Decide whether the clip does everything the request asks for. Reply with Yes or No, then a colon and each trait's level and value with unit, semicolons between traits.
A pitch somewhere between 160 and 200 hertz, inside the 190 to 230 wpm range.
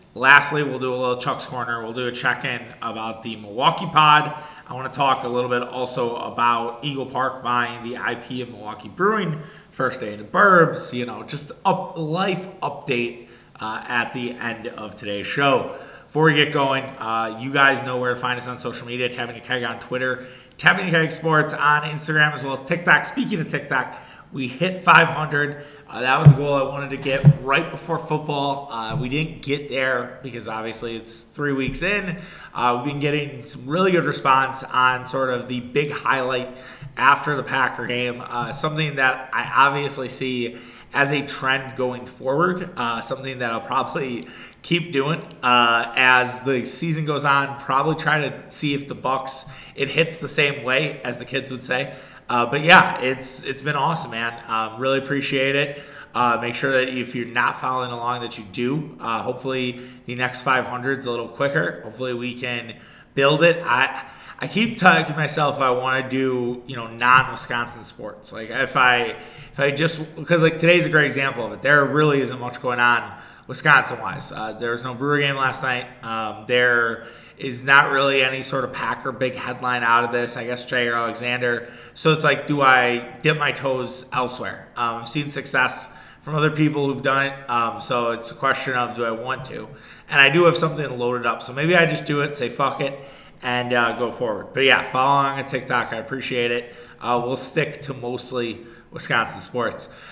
No: low, 130 Hz; average, 200 wpm